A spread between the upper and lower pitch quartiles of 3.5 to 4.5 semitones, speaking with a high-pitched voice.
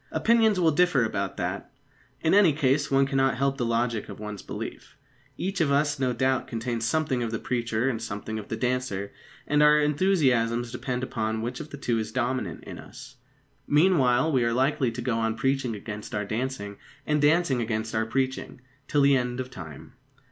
No: average, 3.8 semitones; low, 125 Hz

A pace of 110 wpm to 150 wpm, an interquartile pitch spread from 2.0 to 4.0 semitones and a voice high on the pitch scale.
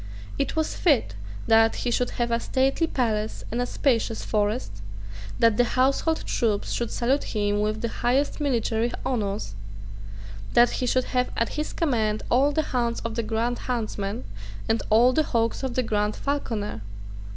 No: average, 165 wpm; average, 2.9 semitones; high, 235 Hz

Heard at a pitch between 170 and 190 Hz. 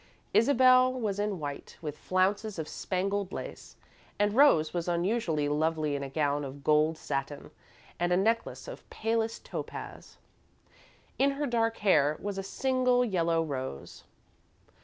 Yes: medium, 185 Hz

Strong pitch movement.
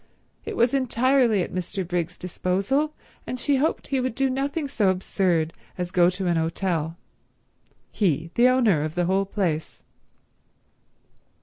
Yes: wide, 6.7 semitones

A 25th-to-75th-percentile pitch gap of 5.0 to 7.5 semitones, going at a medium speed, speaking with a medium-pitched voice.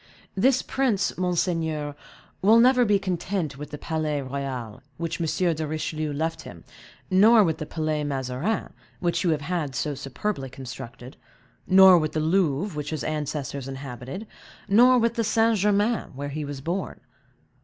Yes: wide, 5.4 semitones; average, 155 wpm; medium, 160 Hz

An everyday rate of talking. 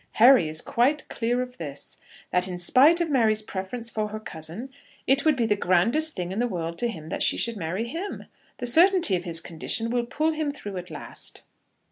No: fast, 210 wpm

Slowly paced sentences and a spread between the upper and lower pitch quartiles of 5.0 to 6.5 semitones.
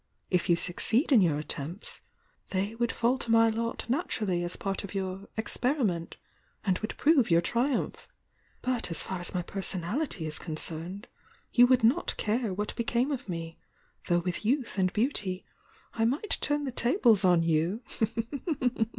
No: average, 160 wpm; wide, 5.5 semitones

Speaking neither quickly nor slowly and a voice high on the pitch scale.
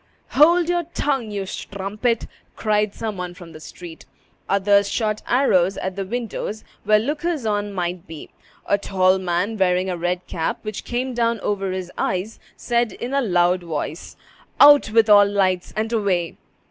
Yes: average, 165 wpm; high, 200 Hz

